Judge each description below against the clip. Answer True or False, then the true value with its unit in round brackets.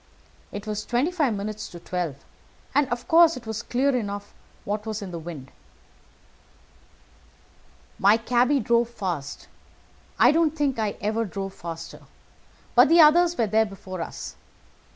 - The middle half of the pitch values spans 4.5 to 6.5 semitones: True (5.0 semitones)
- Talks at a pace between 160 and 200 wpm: False (150 wpm)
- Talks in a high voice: True (220 Hz)